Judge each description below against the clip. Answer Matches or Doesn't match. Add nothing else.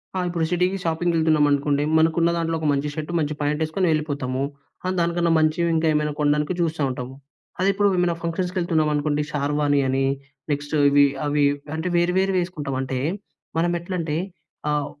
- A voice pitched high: Doesn't match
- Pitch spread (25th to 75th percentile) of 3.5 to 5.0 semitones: Doesn't match